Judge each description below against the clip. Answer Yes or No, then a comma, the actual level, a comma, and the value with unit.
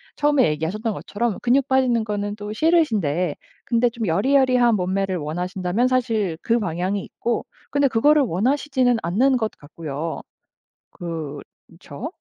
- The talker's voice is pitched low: No, high, 215 Hz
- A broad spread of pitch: Yes, wide, 6.1 semitones